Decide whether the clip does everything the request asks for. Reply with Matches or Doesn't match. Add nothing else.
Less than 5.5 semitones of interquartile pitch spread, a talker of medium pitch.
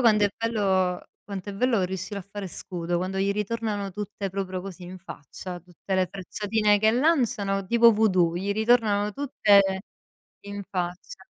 Doesn't match